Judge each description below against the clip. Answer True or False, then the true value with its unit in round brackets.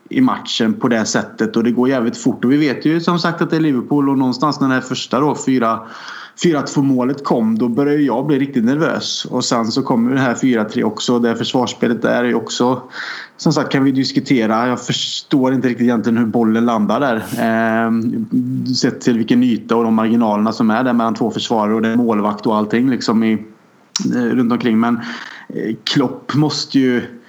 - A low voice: True (125 Hz)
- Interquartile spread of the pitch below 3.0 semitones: False (3.8 semitones)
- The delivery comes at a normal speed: False (210 wpm)